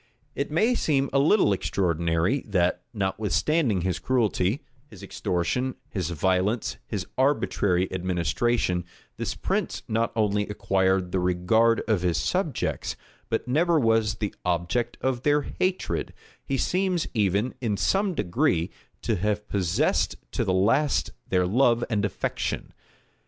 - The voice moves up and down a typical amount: No, wide, 5.8 semitones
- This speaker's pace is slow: Yes, slow, 130 wpm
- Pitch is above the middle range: No, low, 105 Hz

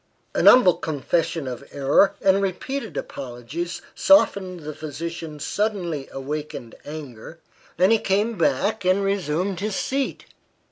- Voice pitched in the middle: Yes, medium, 170 Hz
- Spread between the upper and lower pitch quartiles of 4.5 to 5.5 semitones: Yes, average, 5.2 semitones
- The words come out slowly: Yes, slow, 125 wpm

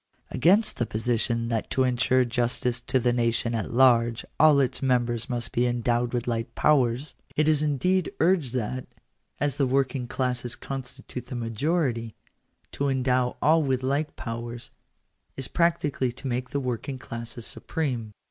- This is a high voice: No, low, 125 Hz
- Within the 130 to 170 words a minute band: Yes, average, 155 wpm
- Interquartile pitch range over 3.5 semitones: No, narrow, 2.6 semitones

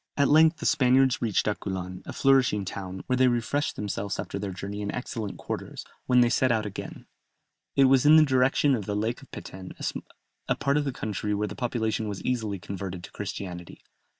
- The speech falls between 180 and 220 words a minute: Yes, average, 200 wpm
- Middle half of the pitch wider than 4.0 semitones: Yes, average, 4.7 semitones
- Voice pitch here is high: No, low, 110 Hz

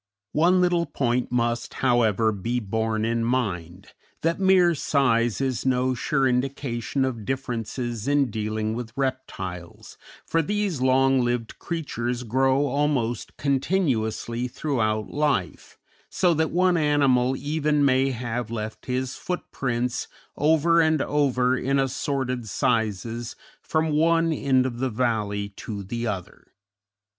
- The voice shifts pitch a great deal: No, average, 3.8 semitones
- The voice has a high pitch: No, low, 125 Hz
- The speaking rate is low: Yes, slow, 125 wpm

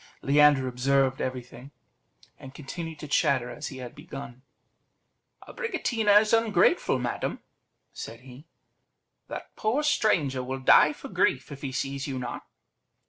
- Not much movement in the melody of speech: No, average, 4.3 semitones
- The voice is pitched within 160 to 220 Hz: No, medium, 140 Hz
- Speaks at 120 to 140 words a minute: Yes, slow, 135 wpm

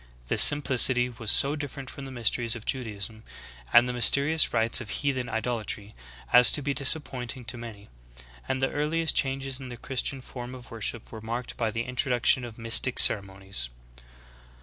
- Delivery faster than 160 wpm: Yes, average, 170 wpm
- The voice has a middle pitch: No, low, 125 Hz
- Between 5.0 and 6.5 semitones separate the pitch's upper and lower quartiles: No, average, 2.8 semitones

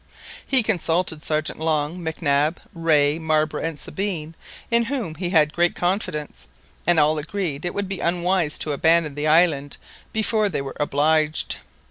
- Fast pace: No, average, 160 wpm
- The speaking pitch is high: No, medium, 160 Hz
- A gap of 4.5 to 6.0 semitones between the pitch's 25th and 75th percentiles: No, average, 2.9 semitones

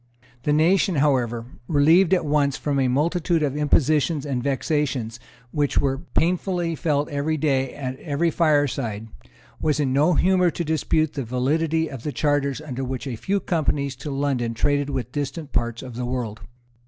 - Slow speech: No, average, 165 wpm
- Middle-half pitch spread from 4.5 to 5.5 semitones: No, average, 3.1 semitones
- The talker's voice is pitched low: No, medium, 145 Hz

